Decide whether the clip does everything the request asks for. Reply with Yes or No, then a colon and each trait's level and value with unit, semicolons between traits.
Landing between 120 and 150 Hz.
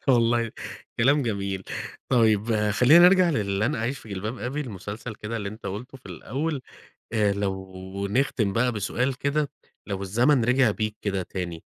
No: low, 110 Hz